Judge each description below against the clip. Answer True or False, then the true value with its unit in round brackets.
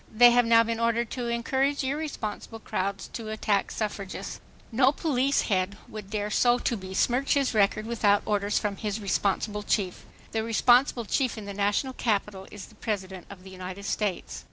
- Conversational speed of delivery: True (175 wpm)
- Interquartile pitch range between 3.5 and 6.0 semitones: False (3.1 semitones)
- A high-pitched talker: True (215 Hz)